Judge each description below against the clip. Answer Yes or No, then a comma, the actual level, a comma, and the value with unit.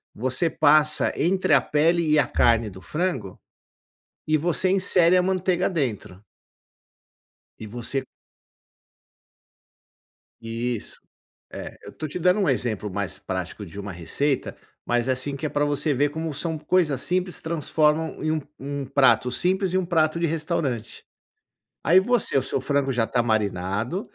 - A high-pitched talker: No, medium, 145 Hz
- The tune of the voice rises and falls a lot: Yes, wide, 6.0 semitones